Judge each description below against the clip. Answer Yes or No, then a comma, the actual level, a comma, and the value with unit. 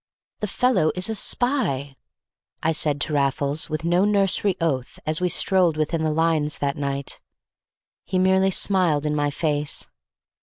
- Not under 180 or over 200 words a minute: No, average, 155 wpm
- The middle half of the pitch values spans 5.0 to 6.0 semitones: No, average, 4.3 semitones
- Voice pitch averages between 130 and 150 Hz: No, medium, 160 Hz